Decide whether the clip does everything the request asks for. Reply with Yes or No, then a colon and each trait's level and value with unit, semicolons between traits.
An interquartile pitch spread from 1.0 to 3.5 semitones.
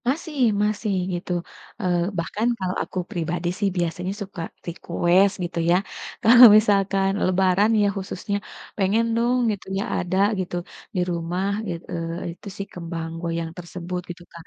Yes: average, 2.8 semitones